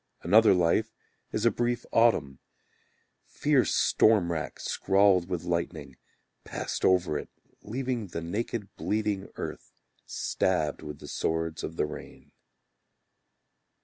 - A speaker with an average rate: No, slow, 115 wpm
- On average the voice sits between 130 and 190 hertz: No, very low, 95 Hz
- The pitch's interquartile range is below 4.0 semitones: No, average, 4.7 semitones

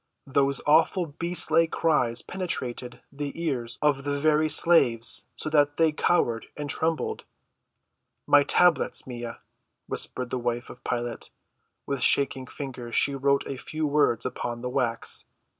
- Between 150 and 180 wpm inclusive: No, average, 140 wpm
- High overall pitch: No, medium, 140 Hz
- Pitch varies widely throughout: No, average, 4.0 semitones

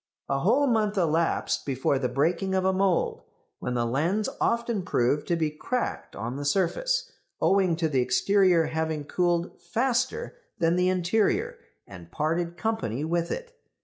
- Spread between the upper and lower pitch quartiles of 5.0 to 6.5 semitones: Yes, wide, 5.4 semitones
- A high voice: No, medium, 170 Hz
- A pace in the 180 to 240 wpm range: No, average, 155 wpm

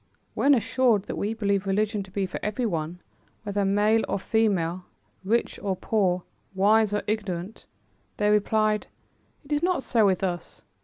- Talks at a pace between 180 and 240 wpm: No, average, 155 wpm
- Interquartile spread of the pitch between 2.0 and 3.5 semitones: Yes, narrow, 2.6 semitones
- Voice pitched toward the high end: Yes, high, 205 Hz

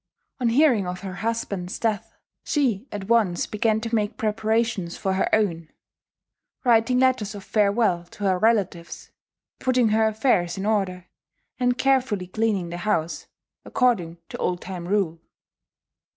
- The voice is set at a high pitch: Yes, high, 210 Hz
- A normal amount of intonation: Yes, average, 4.0 semitones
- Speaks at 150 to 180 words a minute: No, average, 140 wpm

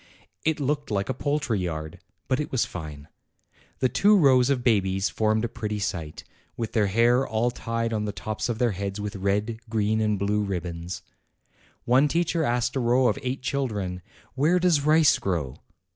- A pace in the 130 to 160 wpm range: No, average, 185 wpm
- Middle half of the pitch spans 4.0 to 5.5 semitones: Yes, average, 4.8 semitones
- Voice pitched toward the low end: Yes, low, 110 Hz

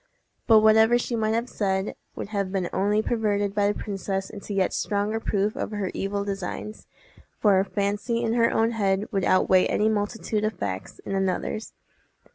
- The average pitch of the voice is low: No, high, 205 Hz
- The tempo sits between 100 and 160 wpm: No, average, 180 wpm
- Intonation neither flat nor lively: No, narrow, 2.0 semitones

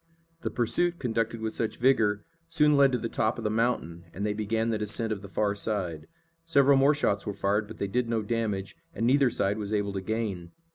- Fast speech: Yes, fast, 225 wpm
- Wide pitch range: No, average, 3.0 semitones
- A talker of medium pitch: No, low, 110 Hz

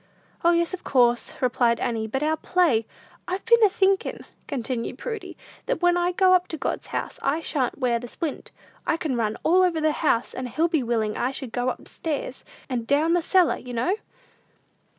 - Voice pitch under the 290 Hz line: No, very high, 300 Hz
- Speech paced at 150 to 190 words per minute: No, average, 200 wpm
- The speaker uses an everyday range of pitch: No, wide, 6.3 semitones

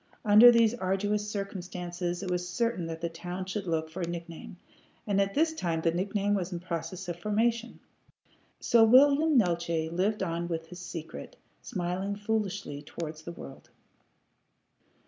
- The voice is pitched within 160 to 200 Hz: Yes, medium, 185 Hz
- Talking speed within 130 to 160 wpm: Yes, average, 155 wpm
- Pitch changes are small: No, average, 3.6 semitones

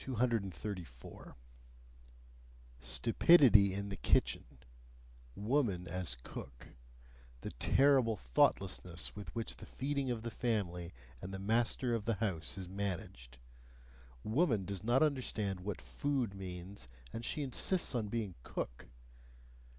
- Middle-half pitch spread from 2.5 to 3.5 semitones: No, average, 4.7 semitones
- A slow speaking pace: Yes, slow, 120 wpm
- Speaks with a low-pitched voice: Yes, low, 100 Hz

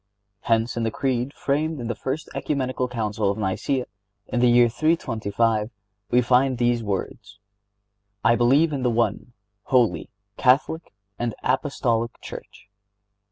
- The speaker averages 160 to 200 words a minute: No, slow, 135 wpm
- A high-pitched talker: No, low, 120 Hz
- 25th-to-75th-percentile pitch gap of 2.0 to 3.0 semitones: Yes, narrow, 2.6 semitones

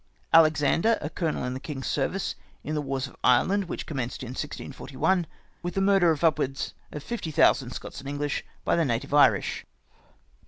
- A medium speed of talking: Yes, average, 190 wpm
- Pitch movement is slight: No, average, 3.9 semitones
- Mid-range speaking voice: Yes, medium, 150 Hz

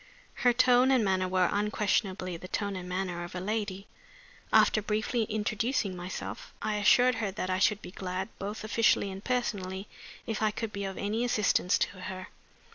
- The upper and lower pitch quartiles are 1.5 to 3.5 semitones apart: Yes, average, 2.8 semitones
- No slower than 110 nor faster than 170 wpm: No, average, 180 wpm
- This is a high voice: Yes, high, 200 Hz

